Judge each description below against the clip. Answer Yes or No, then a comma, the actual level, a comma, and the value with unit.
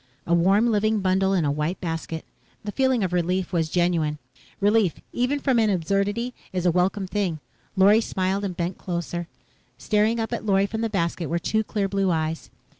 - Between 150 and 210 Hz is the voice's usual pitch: Yes, high, 190 Hz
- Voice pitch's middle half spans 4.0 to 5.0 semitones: No, average, 3.5 semitones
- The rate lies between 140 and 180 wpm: No, average, 190 wpm